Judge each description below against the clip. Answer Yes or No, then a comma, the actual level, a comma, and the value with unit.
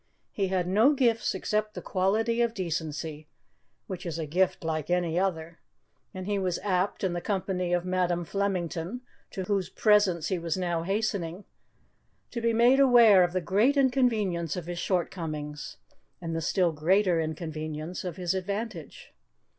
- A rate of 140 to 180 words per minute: Yes, average, 160 wpm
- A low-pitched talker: No, medium, 185 Hz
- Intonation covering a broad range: No, average, 3.6 semitones